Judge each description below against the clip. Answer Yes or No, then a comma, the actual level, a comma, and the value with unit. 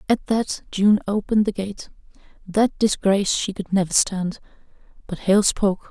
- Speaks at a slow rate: Yes, slow, 130 wpm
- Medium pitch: No, high, 200 Hz